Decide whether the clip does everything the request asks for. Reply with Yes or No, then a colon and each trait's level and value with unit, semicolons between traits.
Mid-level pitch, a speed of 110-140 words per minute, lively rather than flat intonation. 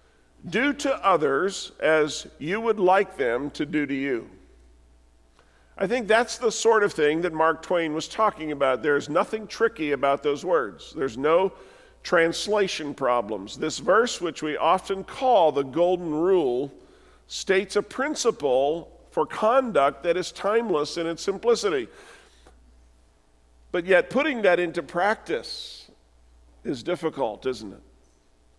Yes: medium, 165 Hz; slow, 135 wpm; wide, 7.3 semitones